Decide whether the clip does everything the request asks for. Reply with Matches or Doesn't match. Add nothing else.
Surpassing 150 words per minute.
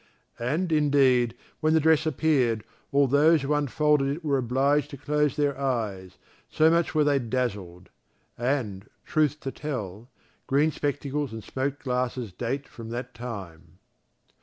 Doesn't match